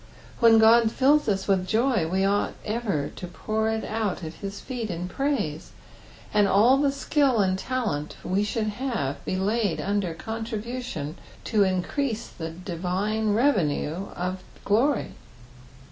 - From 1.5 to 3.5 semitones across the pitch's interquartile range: No, average, 4.2 semitones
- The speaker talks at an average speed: Yes, average, 145 wpm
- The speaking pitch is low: No, high, 210 Hz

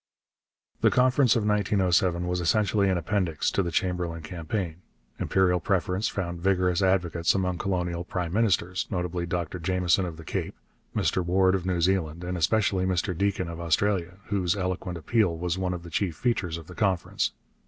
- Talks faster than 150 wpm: Yes, average, 170 wpm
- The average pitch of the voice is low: Yes, very low, 90 Hz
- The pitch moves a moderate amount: No, narrow, 2.0 semitones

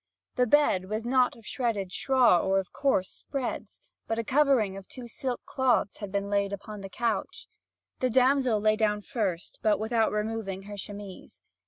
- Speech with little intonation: No, average, 3.8 semitones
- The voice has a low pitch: No, high, 215 Hz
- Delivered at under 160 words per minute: No, average, 175 wpm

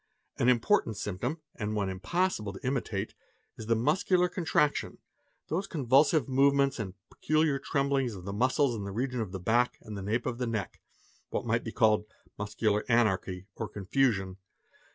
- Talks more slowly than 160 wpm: No, average, 165 wpm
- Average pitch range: Yes, average, 4.9 semitones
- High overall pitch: No, low, 115 Hz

